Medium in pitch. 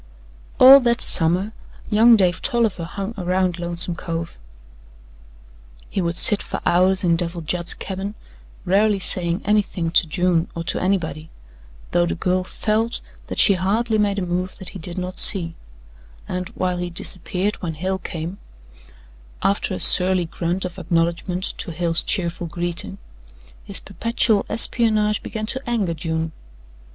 Yes: medium, 180 Hz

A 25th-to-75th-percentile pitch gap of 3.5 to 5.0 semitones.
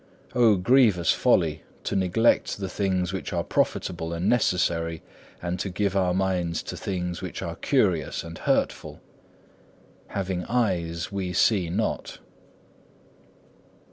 No: narrow, 2.4 semitones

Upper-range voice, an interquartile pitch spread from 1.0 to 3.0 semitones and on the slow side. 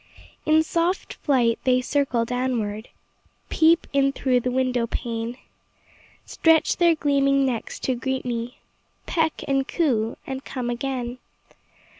Yes: very high, 260 Hz; narrow, 2.6 semitones; slow, 125 wpm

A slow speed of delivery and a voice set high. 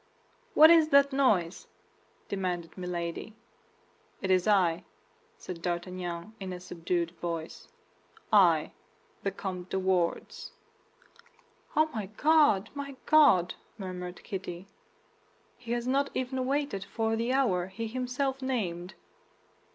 Yes: slow, 115 wpm; high, 195 Hz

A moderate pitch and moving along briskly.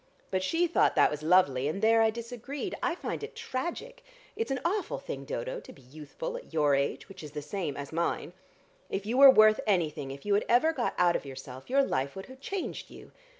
No: high, 210 Hz; fast, 225 wpm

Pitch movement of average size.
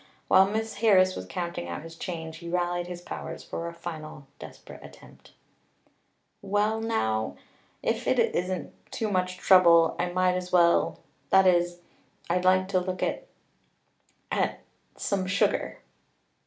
No: narrow, 1.7 semitones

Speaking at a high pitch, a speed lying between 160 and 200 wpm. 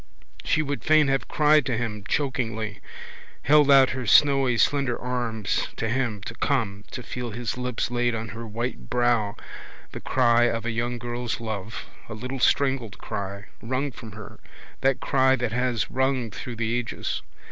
No: low, 120 Hz; average, 170 wpm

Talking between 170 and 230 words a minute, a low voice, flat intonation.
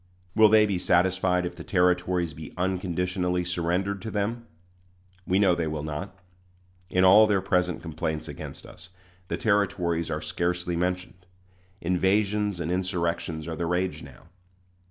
No: average, 145 wpm; very low, 90 Hz; narrow, 1.8 semitones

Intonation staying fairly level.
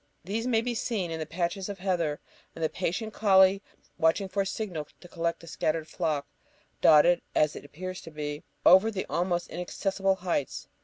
No: average, 3.2 semitones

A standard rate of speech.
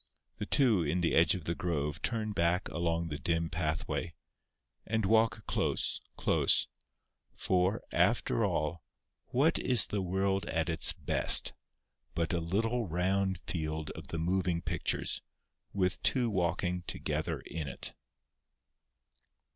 No: slow, 130 wpm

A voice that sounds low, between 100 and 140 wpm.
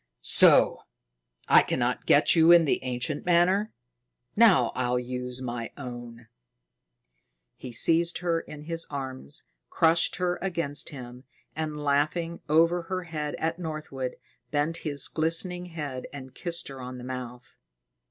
No: medium, 150 Hz; slow, 135 wpm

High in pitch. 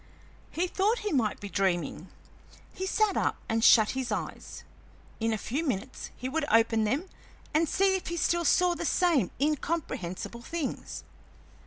Yes: very high, 275 Hz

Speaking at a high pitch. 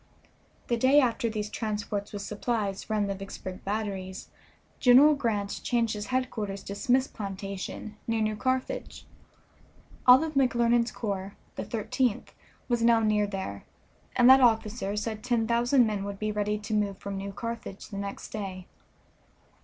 Yes: high, 215 Hz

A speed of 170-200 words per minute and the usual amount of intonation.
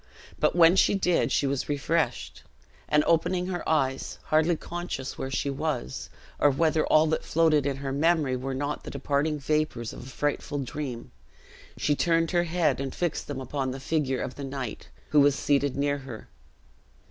Yes: average, 180 wpm; average, 3.1 semitones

